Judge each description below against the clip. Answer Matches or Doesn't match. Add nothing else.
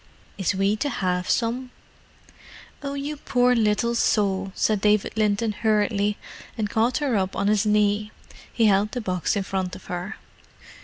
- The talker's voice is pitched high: Matches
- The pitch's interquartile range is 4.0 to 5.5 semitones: Doesn't match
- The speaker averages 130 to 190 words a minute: Matches